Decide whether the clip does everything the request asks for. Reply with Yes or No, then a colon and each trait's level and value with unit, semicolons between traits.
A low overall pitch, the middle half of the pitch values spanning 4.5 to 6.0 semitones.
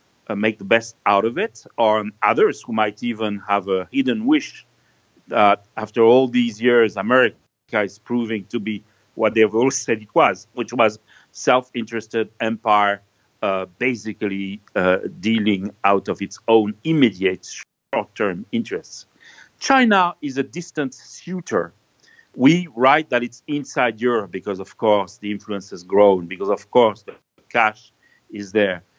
No: low, 110 Hz; average, 3.8 semitones